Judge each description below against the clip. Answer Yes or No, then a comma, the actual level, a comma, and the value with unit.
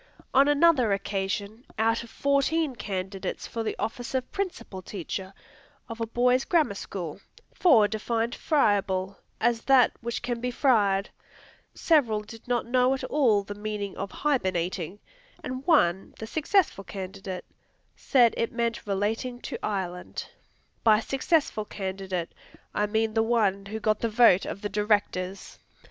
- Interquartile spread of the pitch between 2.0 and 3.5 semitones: No, average, 4.0 semitones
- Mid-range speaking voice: No, high, 220 Hz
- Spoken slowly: No, average, 145 wpm